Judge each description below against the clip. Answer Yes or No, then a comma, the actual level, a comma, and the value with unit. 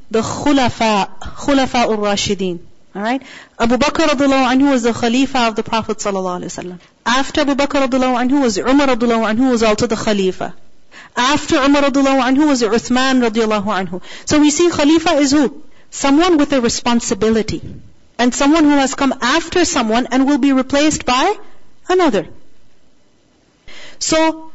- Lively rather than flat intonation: No, average, 4.3 semitones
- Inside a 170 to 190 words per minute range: No, average, 160 wpm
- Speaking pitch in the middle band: No, very high, 255 Hz